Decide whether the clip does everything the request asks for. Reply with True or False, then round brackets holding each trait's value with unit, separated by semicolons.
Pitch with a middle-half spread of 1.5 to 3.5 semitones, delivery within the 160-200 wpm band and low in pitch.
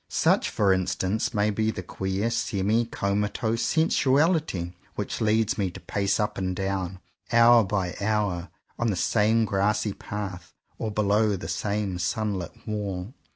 False (2.6 semitones; 145 wpm; 105 Hz)